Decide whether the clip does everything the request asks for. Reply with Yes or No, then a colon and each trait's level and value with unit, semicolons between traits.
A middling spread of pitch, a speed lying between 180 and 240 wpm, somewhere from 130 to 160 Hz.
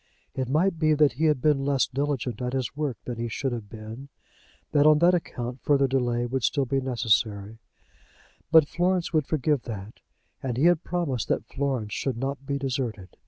Yes: average, 3.8 semitones; average, 190 wpm; low, 135 Hz